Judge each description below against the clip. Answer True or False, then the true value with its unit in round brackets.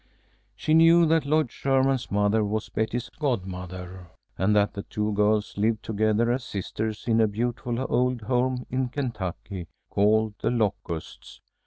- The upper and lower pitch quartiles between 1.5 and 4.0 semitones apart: True (3.6 semitones)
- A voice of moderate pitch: False (110 Hz)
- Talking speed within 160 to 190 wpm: False (145 wpm)